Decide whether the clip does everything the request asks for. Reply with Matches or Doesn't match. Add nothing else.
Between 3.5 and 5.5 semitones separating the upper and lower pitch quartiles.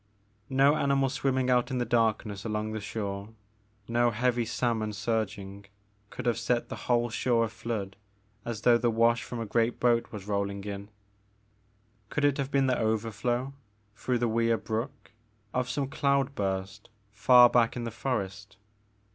Doesn't match